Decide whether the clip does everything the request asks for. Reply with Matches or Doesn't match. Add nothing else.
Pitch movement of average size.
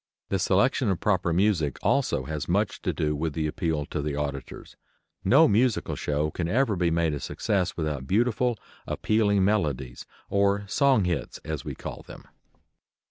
Doesn't match